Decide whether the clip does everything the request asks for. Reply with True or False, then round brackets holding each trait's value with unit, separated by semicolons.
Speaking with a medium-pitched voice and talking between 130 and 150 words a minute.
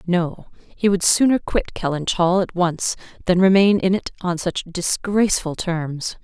False (180 Hz; 165 wpm)